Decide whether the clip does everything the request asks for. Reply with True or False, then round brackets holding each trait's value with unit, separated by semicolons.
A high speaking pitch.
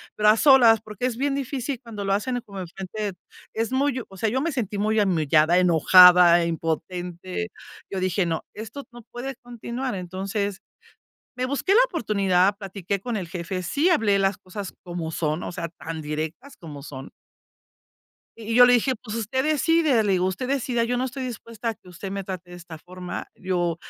True (200 Hz)